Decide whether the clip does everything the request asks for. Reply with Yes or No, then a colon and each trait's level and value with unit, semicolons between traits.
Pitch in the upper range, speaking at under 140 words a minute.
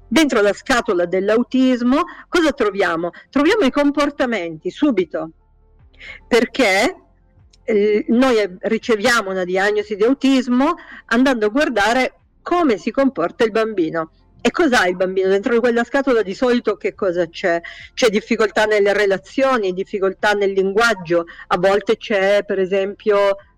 Yes: high, 215 Hz; average, 125 wpm